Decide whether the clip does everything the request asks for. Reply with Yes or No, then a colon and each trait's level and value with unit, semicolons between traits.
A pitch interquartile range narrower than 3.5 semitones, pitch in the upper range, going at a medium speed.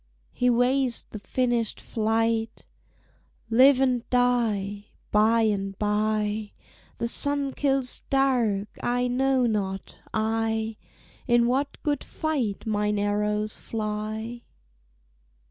No: average, 2.9 semitones; high, 225 Hz; slow, 100 wpm